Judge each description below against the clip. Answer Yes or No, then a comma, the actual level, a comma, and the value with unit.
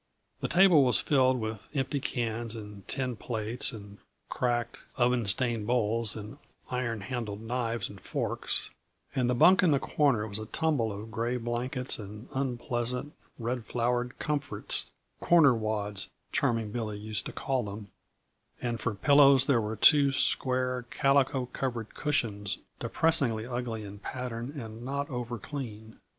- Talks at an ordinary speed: Yes, average, 150 wpm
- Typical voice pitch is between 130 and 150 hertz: No, low, 120 Hz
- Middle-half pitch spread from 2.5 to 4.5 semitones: Yes, average, 3.1 semitones